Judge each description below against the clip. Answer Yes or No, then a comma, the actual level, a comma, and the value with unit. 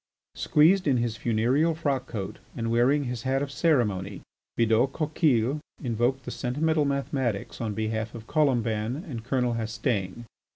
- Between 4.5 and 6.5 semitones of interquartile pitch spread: No, average, 3.8 semitones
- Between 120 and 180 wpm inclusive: Yes, average, 140 wpm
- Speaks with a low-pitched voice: Yes, low, 125 Hz